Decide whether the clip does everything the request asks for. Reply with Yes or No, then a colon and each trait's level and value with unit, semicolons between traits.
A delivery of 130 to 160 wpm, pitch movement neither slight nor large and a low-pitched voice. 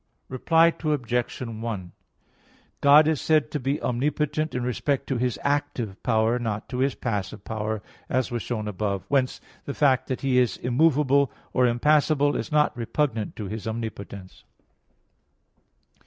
Yes: average, 150 wpm; average, 4.4 semitones; low, 125 Hz